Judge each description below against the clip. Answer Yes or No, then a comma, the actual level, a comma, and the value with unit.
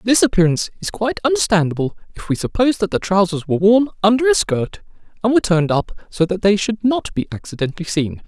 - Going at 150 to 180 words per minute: No, fast, 205 wpm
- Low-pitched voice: No, high, 200 Hz